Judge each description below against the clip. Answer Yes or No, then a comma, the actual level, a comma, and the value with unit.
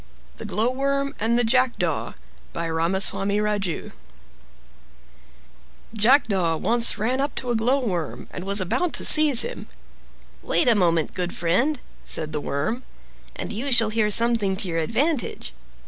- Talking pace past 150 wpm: No, average, 140 wpm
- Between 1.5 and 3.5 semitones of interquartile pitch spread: No, wide, 5.4 semitones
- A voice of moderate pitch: No, high, 220 Hz